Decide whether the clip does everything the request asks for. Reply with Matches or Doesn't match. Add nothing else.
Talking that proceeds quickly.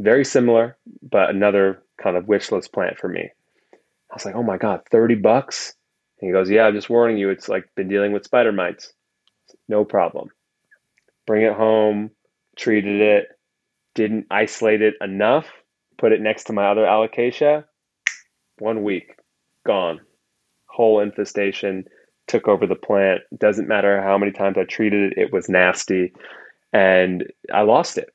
Doesn't match